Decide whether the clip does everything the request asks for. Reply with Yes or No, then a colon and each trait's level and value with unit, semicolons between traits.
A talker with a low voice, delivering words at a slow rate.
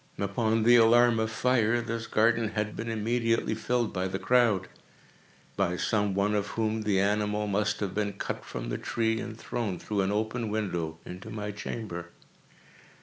No: low, 110 Hz; average, 165 wpm